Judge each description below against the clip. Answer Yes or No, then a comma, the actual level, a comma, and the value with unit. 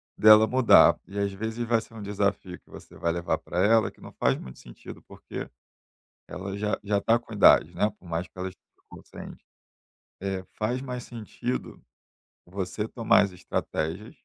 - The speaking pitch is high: No, low, 100 Hz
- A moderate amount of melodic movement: Yes, average, 3.4 semitones